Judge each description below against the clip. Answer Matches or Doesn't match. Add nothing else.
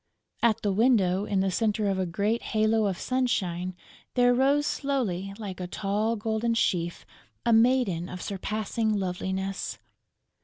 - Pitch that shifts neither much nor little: Matches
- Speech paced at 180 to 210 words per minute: Doesn't match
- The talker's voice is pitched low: Doesn't match